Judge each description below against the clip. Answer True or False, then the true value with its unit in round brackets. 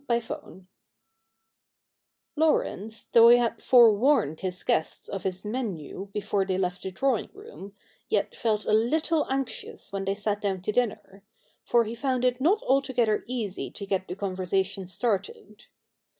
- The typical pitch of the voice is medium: False (210 Hz)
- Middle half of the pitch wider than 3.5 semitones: True (4.2 semitones)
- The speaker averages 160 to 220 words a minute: False (150 wpm)